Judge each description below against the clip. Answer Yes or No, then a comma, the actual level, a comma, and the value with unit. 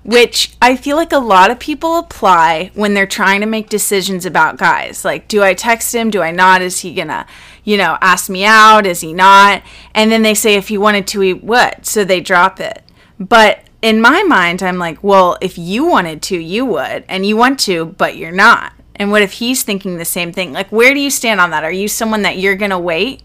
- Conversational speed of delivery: No, fast, 240 wpm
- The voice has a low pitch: No, high, 200 Hz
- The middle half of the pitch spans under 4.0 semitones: Yes, average, 3.3 semitones